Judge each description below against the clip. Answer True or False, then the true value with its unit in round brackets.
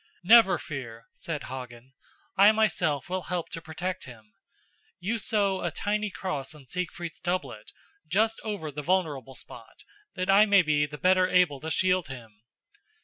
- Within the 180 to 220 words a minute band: False (155 wpm)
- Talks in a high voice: False (175 Hz)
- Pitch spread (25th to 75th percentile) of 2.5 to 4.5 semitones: False (5.1 semitones)